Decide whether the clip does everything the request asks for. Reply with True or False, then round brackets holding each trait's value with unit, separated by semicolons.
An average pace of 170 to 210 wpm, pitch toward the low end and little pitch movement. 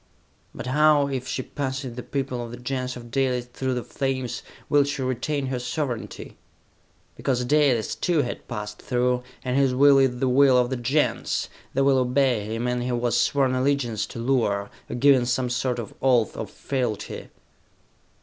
True (180 wpm; 125 Hz; 1.9 semitones)